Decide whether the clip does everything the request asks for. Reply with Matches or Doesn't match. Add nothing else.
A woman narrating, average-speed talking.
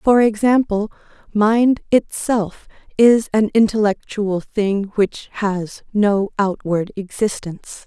Doesn't match